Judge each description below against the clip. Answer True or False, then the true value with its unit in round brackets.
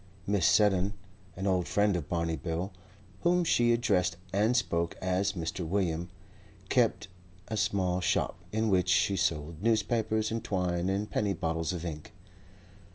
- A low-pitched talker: True (95 Hz)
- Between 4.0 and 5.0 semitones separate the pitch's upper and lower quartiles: False (3.6 semitones)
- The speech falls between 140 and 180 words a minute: True (150 wpm)